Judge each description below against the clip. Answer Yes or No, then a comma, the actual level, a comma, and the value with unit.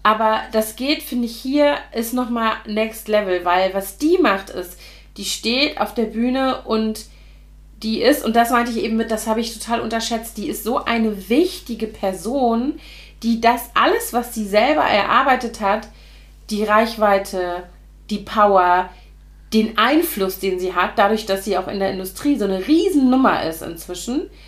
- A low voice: No, high, 220 Hz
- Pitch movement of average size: Yes, average, 3.3 semitones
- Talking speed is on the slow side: No, average, 170 wpm